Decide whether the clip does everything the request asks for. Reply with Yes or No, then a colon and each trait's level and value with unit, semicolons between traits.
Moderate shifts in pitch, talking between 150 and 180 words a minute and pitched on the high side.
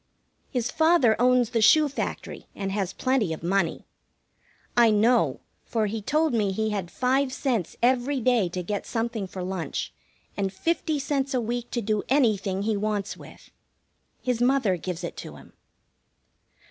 Yes: average, 4.6 semitones; average, 160 wpm; high, 225 Hz